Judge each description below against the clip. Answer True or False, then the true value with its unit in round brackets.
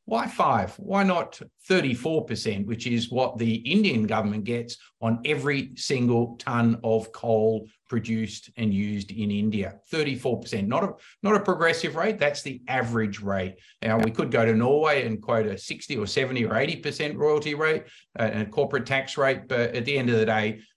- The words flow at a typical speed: True (180 wpm)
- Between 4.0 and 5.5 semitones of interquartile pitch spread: True (4.7 semitones)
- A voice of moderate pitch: False (120 Hz)